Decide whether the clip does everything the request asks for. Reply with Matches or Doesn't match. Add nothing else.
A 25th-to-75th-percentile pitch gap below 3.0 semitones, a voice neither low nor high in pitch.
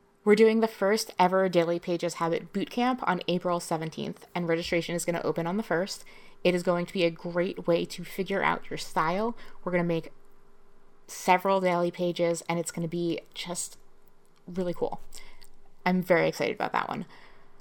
Matches